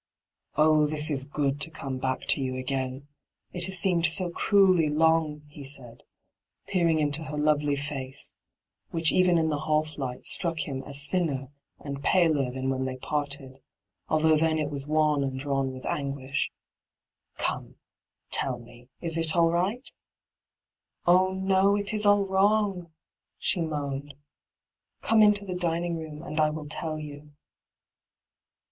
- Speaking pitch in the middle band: Yes, medium, 155 Hz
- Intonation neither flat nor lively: Yes, average, 3.5 semitones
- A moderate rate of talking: Yes, average, 165 wpm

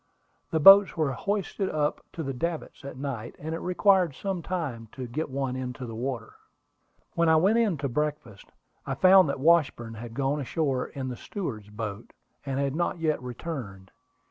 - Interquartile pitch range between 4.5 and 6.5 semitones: Yes, average, 5.1 semitones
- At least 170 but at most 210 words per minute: Yes, average, 180 wpm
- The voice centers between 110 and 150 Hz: Yes, medium, 140 Hz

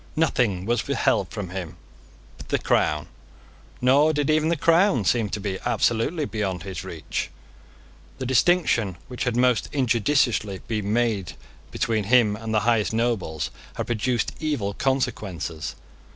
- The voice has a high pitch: No, low, 115 Hz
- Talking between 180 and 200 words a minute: No, average, 140 wpm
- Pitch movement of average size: Yes, average, 4.6 semitones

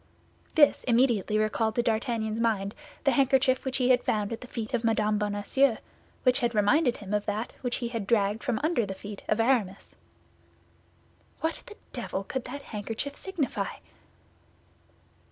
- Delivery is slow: No, average, 160 wpm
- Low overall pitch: No, high, 230 Hz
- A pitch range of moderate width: Yes, average, 3.5 semitones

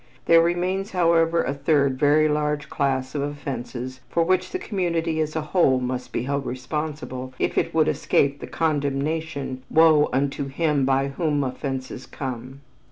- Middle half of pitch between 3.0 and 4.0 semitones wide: Yes, average, 3.3 semitones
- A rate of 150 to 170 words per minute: Yes, average, 160 wpm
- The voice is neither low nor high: Yes, medium, 145 Hz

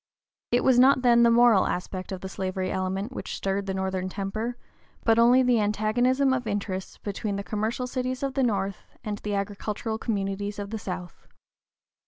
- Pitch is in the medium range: No, high, 210 Hz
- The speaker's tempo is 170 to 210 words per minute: Yes, average, 180 wpm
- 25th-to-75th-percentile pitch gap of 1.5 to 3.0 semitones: No, average, 3.8 semitones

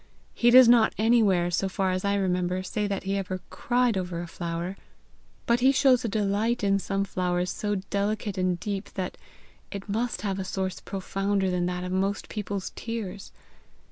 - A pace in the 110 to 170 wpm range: No, average, 180 wpm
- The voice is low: No, high, 195 Hz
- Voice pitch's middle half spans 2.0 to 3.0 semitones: Yes, narrow, 2.5 semitones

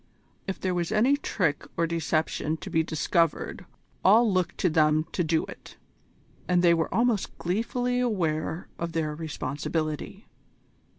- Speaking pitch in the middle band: Yes, medium, 170 Hz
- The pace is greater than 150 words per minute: No, average, 140 wpm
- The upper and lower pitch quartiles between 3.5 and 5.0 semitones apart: Yes, average, 3.8 semitones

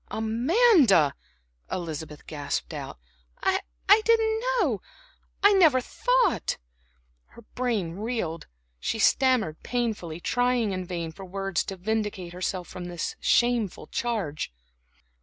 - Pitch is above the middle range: Yes, high, 220 Hz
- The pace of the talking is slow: Yes, slow, 120 wpm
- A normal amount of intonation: No, wide, 6.4 semitones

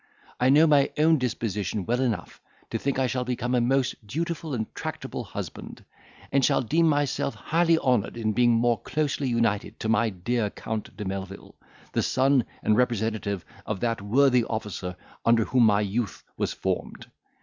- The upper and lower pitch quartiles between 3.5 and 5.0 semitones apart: Yes, average, 3.8 semitones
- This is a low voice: Yes, low, 120 Hz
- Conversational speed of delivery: Yes, average, 170 wpm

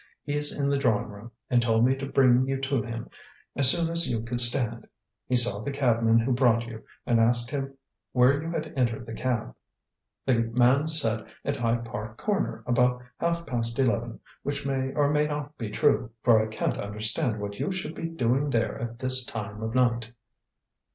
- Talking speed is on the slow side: No, average, 195 wpm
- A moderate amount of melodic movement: Yes, average, 3.4 semitones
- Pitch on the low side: Yes, low, 125 Hz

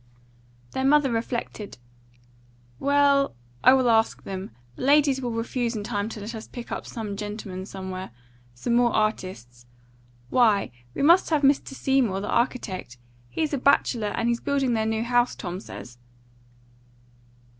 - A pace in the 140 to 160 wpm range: Yes, average, 145 wpm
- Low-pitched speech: No, high, 230 Hz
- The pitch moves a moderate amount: Yes, average, 4.6 semitones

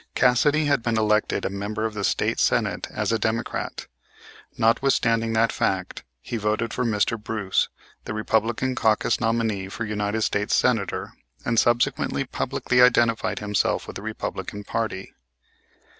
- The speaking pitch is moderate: No, low, 110 Hz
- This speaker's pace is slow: No, average, 145 wpm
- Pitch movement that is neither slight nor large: No, narrow, 1.8 semitones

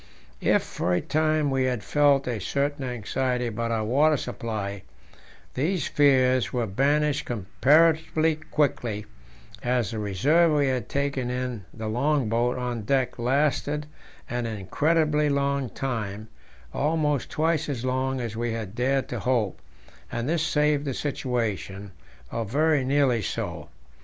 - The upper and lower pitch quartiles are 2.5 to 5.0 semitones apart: Yes, average, 4.2 semitones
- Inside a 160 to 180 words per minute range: No, average, 140 wpm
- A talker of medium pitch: No, low, 130 Hz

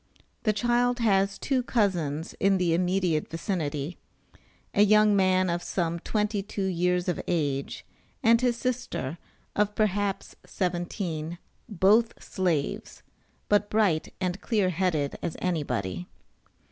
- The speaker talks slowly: Yes, slow, 120 wpm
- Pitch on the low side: No, medium, 185 Hz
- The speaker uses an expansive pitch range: No, average, 3.9 semitones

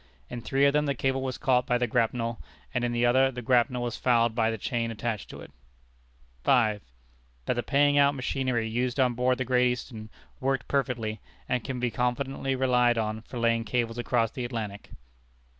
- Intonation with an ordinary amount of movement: No, narrow, 2.1 semitones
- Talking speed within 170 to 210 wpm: Yes, average, 195 wpm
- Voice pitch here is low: Yes, low, 125 Hz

